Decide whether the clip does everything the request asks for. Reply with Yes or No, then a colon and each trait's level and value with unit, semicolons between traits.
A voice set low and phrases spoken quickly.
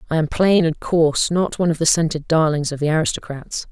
No: medium, 160 Hz; fast, 225 wpm